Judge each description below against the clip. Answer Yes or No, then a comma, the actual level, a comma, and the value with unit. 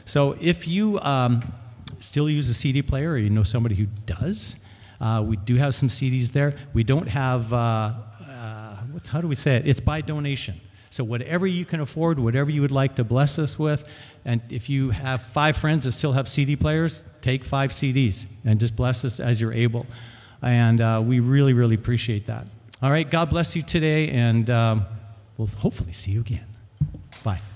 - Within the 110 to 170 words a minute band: No, average, 195 wpm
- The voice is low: Yes, low, 125 Hz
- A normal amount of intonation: Yes, average, 4.2 semitones